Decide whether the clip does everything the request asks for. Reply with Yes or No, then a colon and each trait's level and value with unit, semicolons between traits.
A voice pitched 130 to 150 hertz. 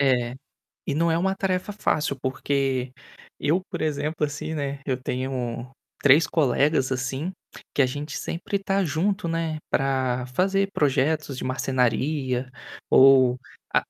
Yes: medium, 140 Hz